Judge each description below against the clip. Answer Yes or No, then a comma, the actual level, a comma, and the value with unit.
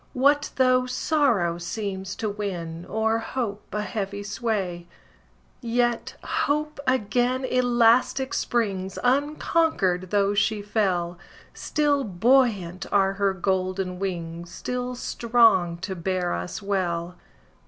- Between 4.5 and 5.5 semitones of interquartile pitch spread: Yes, average, 5.0 semitones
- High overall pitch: Yes, high, 205 Hz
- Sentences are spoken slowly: Yes, slow, 110 wpm